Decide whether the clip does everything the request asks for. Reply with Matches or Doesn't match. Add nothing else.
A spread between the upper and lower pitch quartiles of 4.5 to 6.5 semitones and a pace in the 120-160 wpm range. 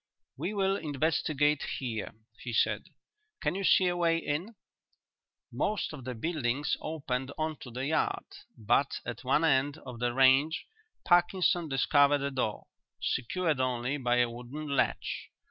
Doesn't match